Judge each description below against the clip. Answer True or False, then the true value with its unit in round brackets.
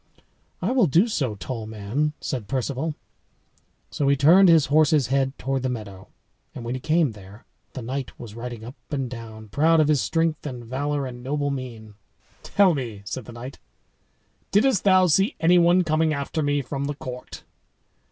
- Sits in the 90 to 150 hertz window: True (135 Hz)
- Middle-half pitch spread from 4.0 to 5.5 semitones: True (4.5 semitones)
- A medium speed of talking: True (180 wpm)